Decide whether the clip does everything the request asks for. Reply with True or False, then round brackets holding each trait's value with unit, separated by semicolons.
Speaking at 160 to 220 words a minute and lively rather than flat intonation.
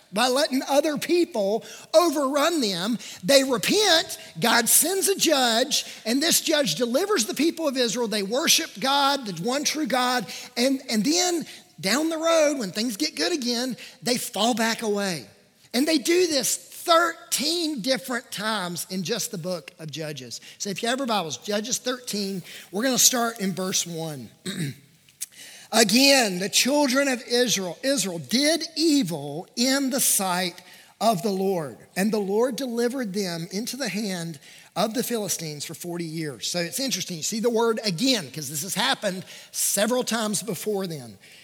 True (165 wpm; 6.2 semitones)